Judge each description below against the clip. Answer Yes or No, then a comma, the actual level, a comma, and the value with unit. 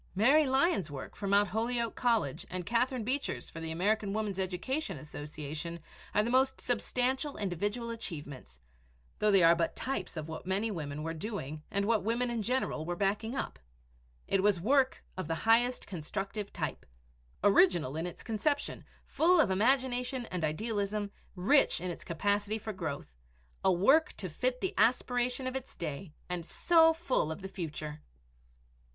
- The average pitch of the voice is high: Yes, high, 205 Hz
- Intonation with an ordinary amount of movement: No, wide, 6.3 semitones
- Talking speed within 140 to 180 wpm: Yes, average, 165 wpm